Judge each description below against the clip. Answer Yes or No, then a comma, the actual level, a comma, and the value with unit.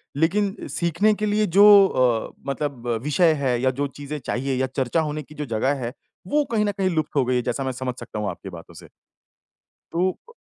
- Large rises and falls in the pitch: Yes, wide, 5.9 semitones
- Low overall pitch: No, medium, 145 Hz